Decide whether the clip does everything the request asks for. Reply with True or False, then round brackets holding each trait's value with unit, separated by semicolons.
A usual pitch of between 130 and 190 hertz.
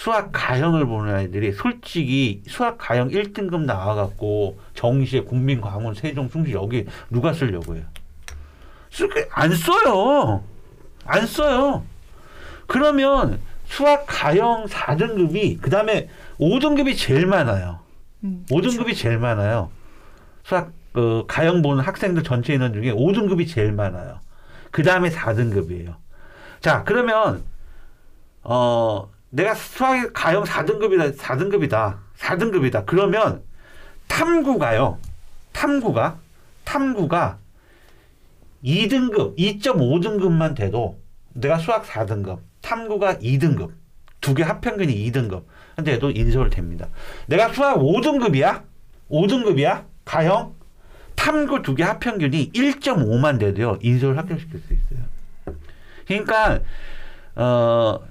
True (135 Hz)